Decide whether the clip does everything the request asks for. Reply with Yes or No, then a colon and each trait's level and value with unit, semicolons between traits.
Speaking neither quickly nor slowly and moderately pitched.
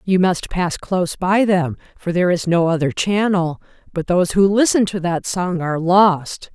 Yes: average, 195 wpm; medium, 180 Hz